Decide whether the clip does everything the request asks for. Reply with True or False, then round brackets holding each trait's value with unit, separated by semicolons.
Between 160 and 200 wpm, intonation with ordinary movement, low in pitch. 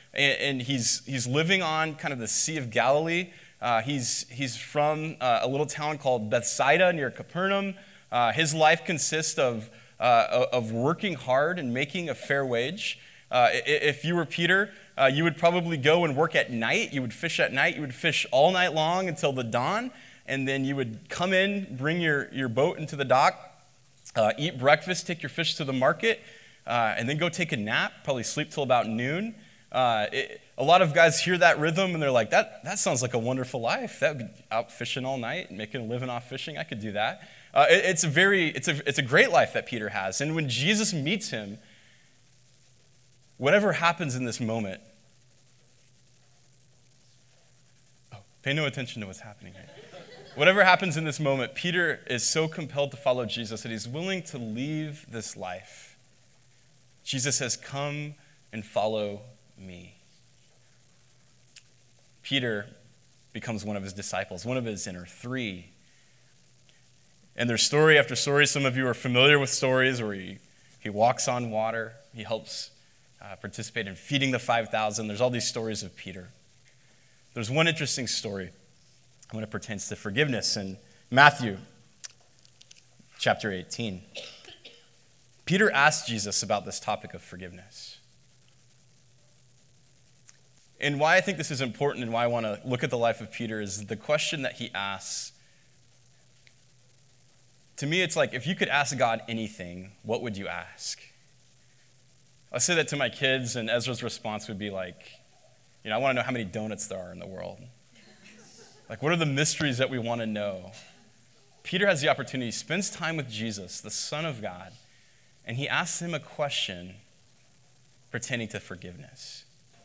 True (175 wpm; 4.5 semitones; 130 Hz)